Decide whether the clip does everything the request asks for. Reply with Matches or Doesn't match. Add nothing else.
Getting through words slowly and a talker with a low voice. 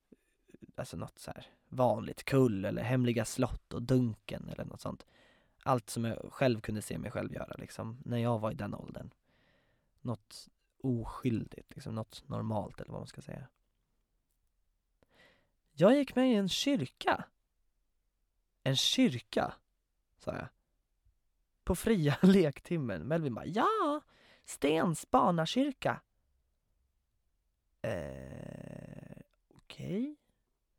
Matches